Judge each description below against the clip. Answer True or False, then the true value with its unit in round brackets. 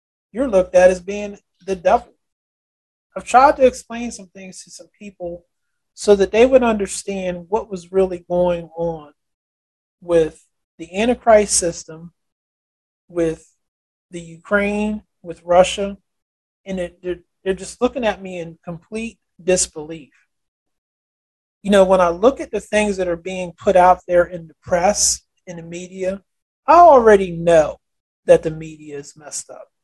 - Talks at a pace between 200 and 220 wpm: False (150 wpm)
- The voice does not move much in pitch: False (3.3 semitones)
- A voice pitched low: False (185 Hz)